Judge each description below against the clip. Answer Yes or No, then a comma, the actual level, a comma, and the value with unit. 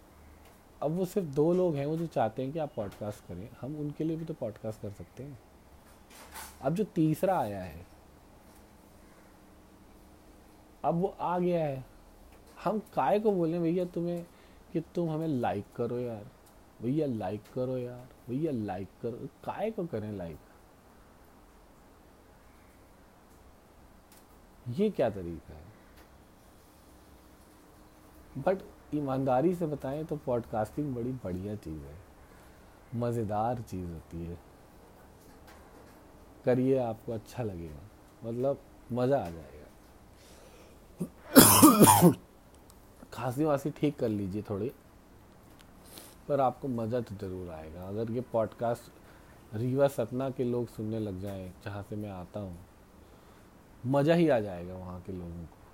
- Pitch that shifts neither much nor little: No, wide, 7.2 semitones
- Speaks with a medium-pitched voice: No, low, 110 Hz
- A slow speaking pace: Yes, slow, 125 wpm